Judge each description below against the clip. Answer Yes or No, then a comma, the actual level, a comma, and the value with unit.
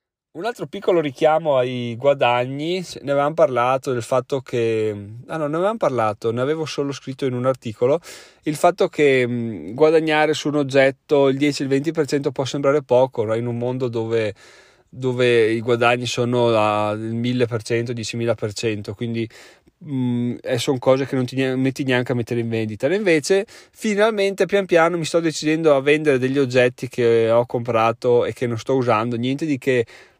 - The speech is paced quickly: Yes, fast, 175 wpm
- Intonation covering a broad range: No, average, 3.9 semitones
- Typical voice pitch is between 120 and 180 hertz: Yes, low, 130 Hz